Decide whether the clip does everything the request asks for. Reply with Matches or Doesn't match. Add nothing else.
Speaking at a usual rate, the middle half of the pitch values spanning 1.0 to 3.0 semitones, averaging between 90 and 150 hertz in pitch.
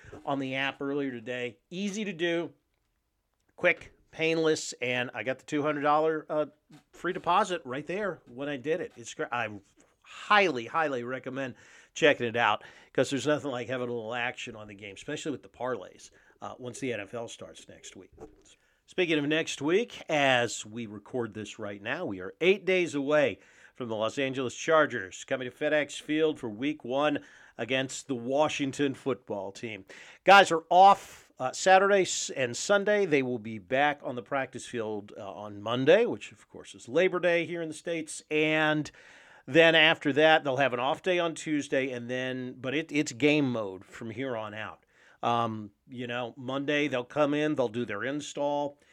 Doesn't match